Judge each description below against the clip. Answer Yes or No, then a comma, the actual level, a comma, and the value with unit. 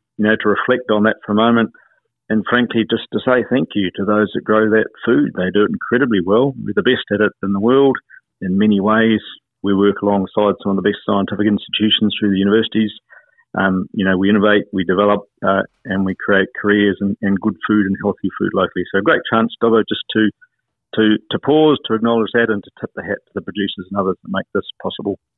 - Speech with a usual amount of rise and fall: No, narrow, 1.8 semitones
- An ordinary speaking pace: No, fast, 225 wpm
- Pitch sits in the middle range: No, low, 105 Hz